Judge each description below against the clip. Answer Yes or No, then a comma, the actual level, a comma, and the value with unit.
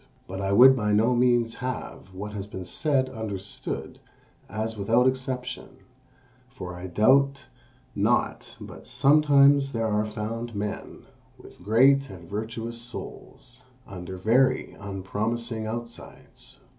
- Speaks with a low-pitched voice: Yes, low, 115 Hz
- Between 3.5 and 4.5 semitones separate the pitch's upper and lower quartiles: Yes, average, 3.8 semitones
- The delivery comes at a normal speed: No, slow, 120 wpm